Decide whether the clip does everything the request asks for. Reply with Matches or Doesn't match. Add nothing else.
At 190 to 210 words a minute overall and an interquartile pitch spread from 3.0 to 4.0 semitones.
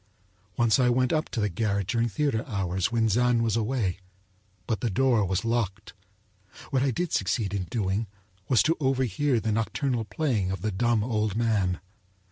Doesn't match